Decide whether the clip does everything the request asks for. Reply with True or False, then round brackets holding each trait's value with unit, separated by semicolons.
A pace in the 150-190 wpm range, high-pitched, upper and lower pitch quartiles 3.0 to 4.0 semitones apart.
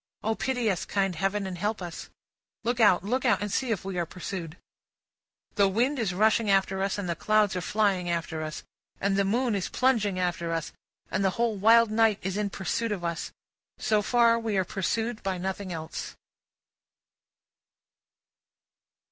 True (180 wpm; 200 Hz; 3.4 semitones)